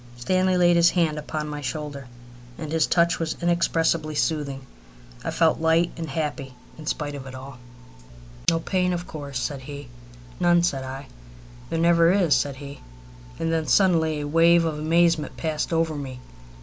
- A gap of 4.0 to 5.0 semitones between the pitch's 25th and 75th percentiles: No, average, 2.7 semitones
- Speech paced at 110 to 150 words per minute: No, average, 165 wpm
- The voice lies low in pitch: No, medium, 160 Hz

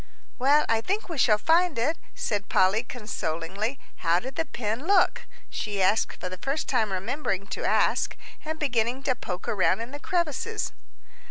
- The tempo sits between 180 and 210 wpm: No, average, 170 wpm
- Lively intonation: Yes, wide, 6.7 semitones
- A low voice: No, high, 235 Hz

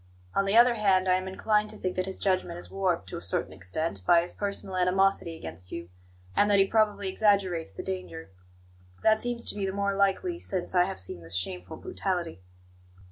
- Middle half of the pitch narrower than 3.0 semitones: No, average, 3.6 semitones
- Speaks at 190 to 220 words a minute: Yes, fast, 205 wpm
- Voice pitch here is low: No, medium, 185 Hz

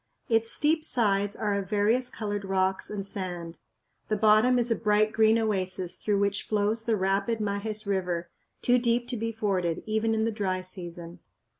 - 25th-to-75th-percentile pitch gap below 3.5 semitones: Yes, average, 2.7 semitones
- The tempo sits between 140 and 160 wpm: No, average, 175 wpm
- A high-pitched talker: Yes, high, 210 Hz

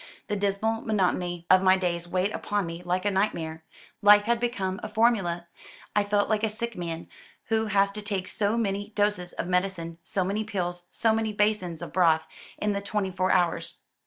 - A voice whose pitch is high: Yes, high, 195 Hz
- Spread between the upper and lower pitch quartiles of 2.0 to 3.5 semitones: Yes, average, 2.9 semitones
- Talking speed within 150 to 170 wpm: No, average, 190 wpm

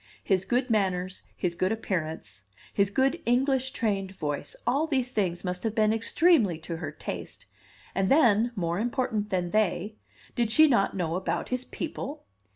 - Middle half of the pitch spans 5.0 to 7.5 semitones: Yes, wide, 5.5 semitones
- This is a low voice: No, high, 210 Hz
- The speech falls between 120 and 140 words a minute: No, average, 160 wpm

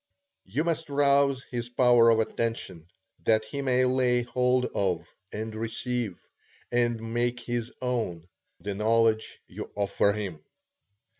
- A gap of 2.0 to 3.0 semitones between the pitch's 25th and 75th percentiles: Yes, narrow, 2.5 semitones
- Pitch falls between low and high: No, low, 120 Hz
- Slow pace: Yes, slow, 130 wpm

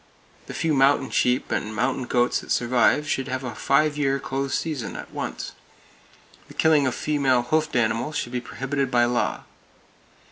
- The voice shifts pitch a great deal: No, average, 2.8 semitones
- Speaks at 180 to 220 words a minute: No, average, 170 wpm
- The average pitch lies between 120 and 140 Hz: Yes, low, 135 Hz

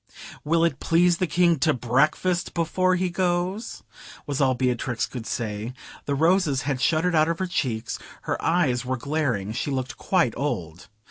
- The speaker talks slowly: No, average, 170 wpm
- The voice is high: No, medium, 150 Hz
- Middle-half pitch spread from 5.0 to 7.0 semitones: Yes, wide, 5.6 semitones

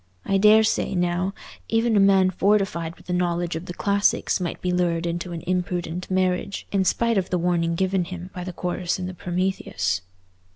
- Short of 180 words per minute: No, average, 190 wpm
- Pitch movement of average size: No, narrow, 1.8 semitones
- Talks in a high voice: No, medium, 180 Hz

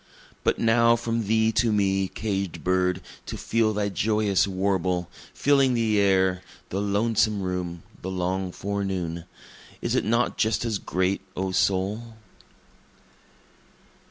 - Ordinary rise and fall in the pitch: Yes, average, 3.0 semitones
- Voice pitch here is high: No, low, 100 Hz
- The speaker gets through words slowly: Yes, slow, 130 wpm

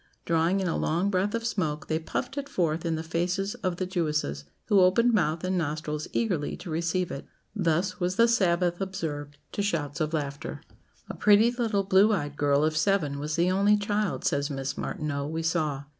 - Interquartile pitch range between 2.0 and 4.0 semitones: No, average, 4.4 semitones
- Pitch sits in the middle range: Yes, medium, 170 Hz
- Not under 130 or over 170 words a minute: No, average, 195 wpm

